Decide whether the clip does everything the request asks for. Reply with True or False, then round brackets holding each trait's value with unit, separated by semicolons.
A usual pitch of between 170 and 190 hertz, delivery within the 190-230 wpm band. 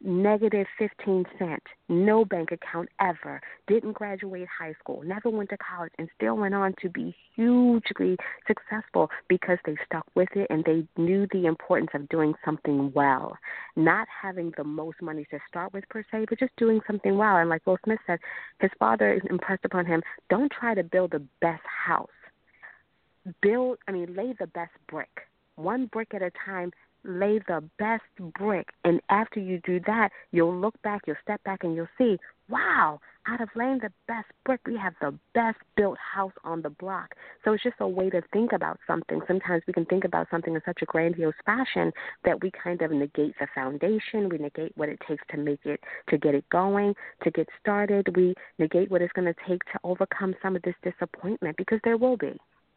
True (185 Hz; 200 wpm)